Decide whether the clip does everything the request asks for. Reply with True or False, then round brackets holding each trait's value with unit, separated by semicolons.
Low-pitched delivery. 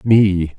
True (95 Hz)